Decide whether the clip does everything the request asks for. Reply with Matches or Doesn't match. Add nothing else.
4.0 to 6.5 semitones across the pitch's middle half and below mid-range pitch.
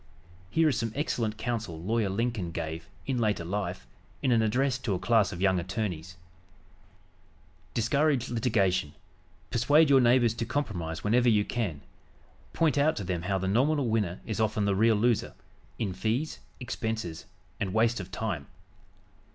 Matches